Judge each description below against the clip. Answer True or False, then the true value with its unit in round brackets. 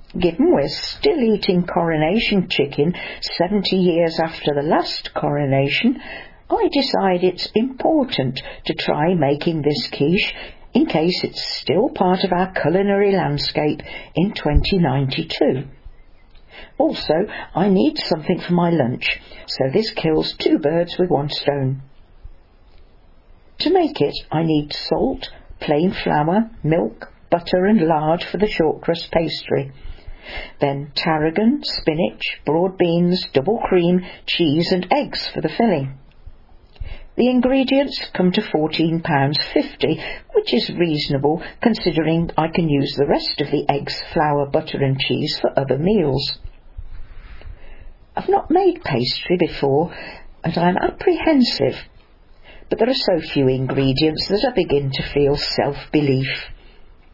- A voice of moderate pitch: True (165 Hz)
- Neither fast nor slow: False (130 wpm)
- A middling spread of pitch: False (5.7 semitones)